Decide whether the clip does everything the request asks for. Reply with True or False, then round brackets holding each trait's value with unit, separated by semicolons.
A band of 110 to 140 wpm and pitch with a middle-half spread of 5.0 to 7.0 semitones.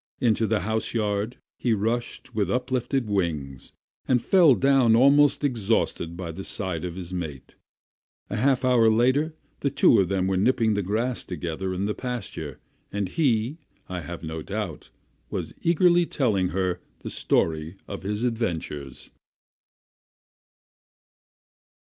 True (135 wpm; 5.5 semitones)